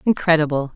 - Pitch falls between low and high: Yes, medium, 160 Hz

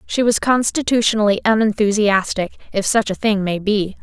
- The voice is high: Yes, high, 210 Hz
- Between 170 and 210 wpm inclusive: No, average, 150 wpm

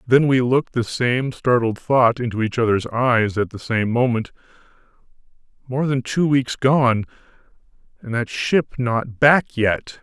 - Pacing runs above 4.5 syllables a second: No, 4.2 syllables/s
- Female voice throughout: No, male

